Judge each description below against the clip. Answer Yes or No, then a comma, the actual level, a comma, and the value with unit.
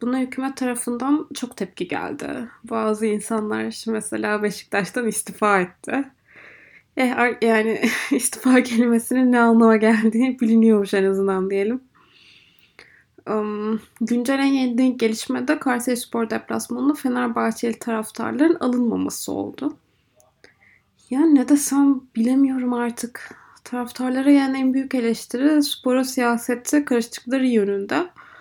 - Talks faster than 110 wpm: No, average, 105 wpm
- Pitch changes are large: No, average, 2.8 semitones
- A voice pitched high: Yes, high, 245 Hz